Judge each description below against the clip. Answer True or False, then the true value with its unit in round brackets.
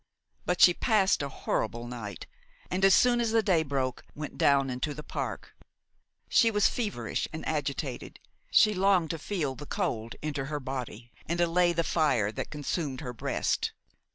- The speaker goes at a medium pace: True (170 wpm)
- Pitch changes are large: True (6.0 semitones)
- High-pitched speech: False (155 Hz)